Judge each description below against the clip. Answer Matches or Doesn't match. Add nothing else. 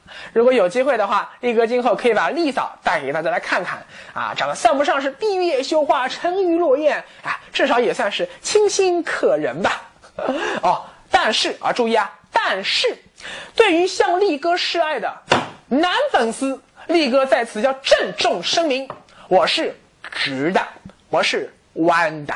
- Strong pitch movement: Matches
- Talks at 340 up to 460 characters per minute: Doesn't match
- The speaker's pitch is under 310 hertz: Doesn't match